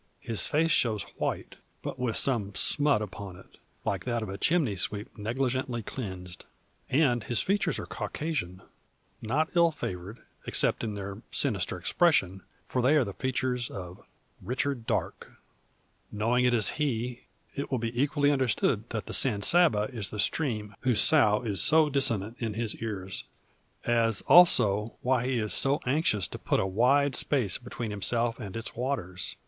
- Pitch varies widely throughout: No, average, 4.6 semitones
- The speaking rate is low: No, average, 165 wpm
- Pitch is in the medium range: No, low, 120 Hz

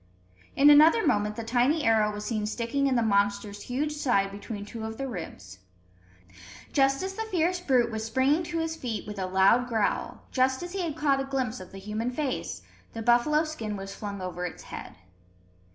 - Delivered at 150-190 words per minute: No, average, 200 wpm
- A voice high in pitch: Yes, high, 240 Hz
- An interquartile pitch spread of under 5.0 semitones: No, wide, 5.5 semitones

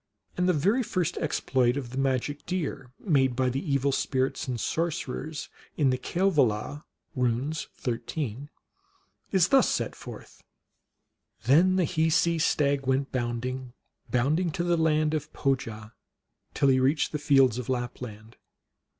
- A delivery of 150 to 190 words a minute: No, average, 140 wpm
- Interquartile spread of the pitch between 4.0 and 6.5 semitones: No, average, 3.6 semitones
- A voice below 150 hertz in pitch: Yes, medium, 140 Hz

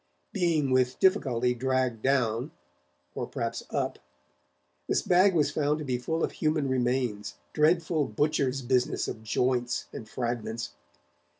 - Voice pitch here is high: No, low, 130 Hz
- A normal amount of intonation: Yes, average, 4.0 semitones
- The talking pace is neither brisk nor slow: No, slow, 130 wpm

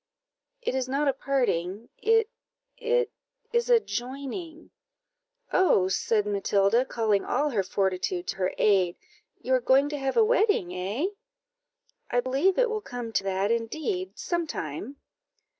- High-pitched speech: Yes, very high, 260 Hz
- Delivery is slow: No, average, 145 wpm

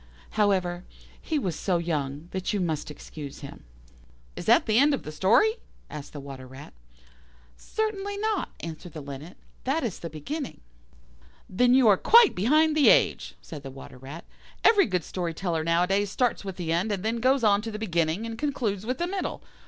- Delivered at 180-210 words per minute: Yes, average, 190 wpm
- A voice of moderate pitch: No, high, 195 Hz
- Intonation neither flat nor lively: No, wide, 8.1 semitones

